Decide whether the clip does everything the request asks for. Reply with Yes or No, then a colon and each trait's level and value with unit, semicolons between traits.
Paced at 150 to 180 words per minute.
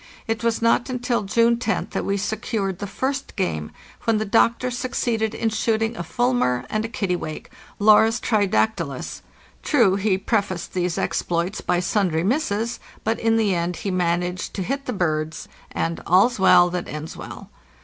Yes: average, 170 wpm